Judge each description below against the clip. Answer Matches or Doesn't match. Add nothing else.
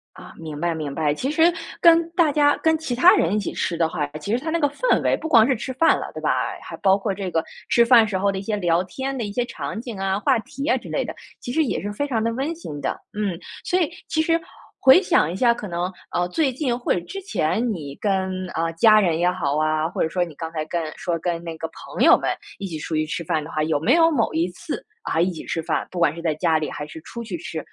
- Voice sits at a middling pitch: Doesn't match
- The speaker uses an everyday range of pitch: Doesn't match